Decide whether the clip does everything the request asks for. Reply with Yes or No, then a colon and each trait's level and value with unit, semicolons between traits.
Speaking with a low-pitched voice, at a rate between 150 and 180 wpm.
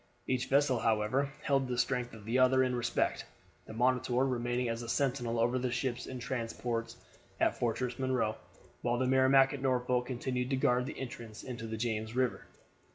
Yes: low, 125 Hz; average, 175 wpm